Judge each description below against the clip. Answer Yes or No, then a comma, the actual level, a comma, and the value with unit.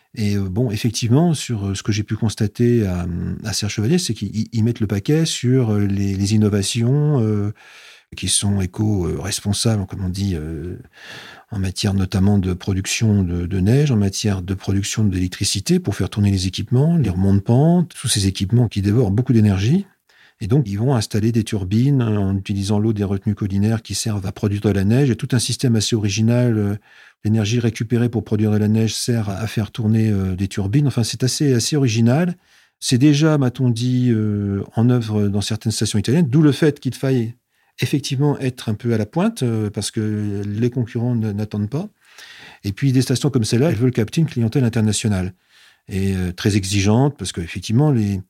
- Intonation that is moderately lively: Yes, average, 3.6 semitones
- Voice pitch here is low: Yes, low, 110 Hz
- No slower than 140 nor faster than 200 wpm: Yes, average, 190 wpm